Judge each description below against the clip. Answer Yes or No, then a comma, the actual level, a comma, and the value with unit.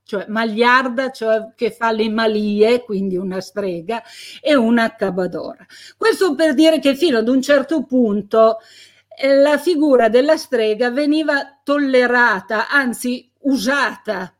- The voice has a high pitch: Yes, high, 245 Hz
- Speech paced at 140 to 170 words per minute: No, average, 130 wpm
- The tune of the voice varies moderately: Yes, average, 4.2 semitones